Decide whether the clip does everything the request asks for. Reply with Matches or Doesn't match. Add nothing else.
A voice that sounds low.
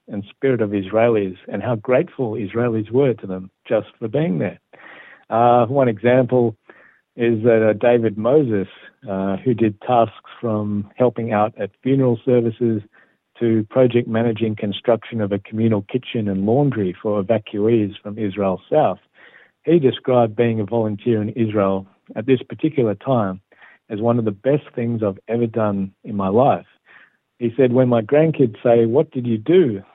Matches